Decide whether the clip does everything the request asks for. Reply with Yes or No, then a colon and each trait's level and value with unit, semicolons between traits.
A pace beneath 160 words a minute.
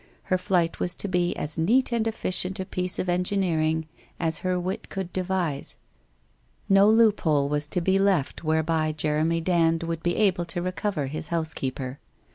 No: average, 170 wpm